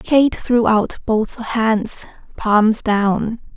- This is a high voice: Yes, high, 220 Hz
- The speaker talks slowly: Yes, slow, 120 wpm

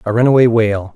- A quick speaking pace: No, average, 190 wpm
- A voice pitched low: Yes, low, 115 Hz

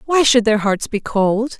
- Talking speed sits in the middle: No, fast, 225 wpm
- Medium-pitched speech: No, high, 230 Hz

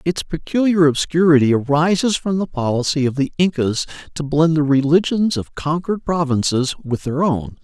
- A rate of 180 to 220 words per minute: No, average, 155 wpm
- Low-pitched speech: No, medium, 155 Hz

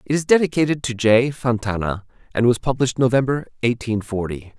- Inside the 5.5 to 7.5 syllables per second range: Yes, 5.8 syllables/s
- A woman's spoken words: No, male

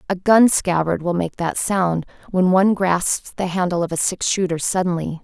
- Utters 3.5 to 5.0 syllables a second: Yes, 4.8 syllables/s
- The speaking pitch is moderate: Yes, medium, 180 Hz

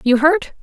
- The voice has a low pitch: No, very high, 300 Hz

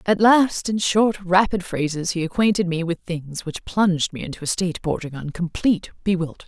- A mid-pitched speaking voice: Yes, medium, 180 Hz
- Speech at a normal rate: Yes, average, 195 wpm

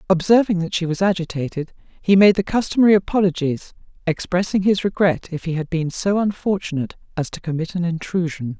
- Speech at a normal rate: Yes, average, 170 wpm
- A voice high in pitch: No, medium, 180 Hz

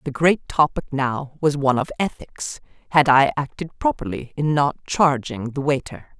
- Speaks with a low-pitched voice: No, medium, 145 Hz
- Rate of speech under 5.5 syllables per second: Yes, 4.7 syllables/s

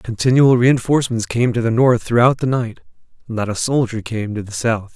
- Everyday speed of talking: Yes, average, 195 wpm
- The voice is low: Yes, low, 120 Hz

